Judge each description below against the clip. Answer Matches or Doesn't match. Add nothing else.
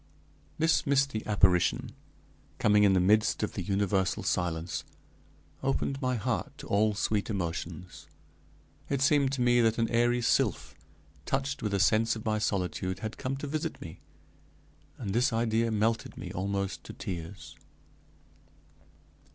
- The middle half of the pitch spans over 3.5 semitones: Matches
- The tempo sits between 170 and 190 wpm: Doesn't match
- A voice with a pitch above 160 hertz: Doesn't match